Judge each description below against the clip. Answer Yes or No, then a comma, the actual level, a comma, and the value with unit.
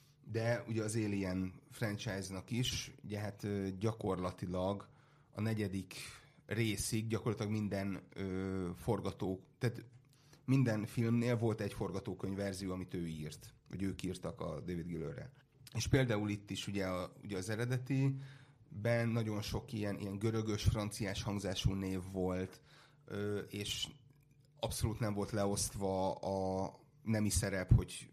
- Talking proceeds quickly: No, average, 130 wpm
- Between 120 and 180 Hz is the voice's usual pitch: No, low, 105 Hz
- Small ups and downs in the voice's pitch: No, average, 3.6 semitones